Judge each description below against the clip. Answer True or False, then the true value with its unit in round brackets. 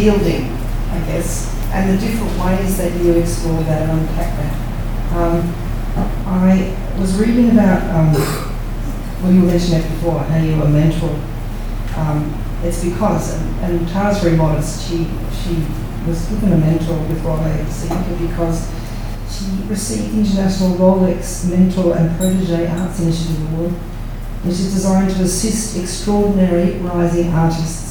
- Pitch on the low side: False (165 Hz)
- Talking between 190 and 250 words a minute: False (140 wpm)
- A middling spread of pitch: True (3.4 semitones)